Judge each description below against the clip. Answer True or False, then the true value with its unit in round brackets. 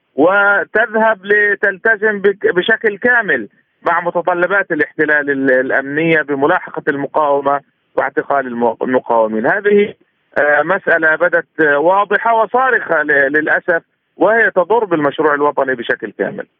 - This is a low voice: False (170 Hz)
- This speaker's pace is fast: False (85 wpm)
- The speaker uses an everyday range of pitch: False (6.2 semitones)